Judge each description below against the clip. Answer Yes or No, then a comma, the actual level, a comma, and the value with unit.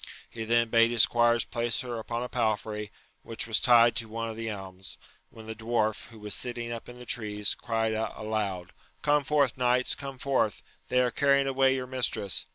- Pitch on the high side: No, low, 115 Hz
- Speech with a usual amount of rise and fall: No, narrow, 2.2 semitones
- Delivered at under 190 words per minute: No, fast, 205 wpm